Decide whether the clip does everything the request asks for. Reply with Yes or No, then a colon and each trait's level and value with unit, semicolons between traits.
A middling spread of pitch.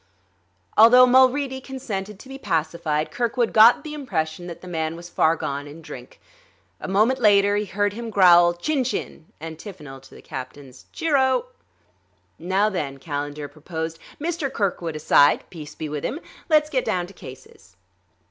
No: wide, 7.9 semitones